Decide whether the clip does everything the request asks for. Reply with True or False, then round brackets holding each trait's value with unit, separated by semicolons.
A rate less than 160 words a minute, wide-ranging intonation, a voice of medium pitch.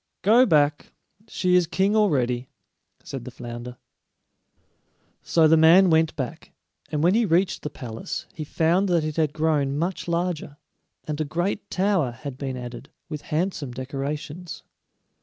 False (150 wpm; 4.5 semitones; 155 Hz)